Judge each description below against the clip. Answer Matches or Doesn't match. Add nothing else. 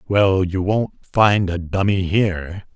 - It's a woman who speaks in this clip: Doesn't match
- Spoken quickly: Doesn't match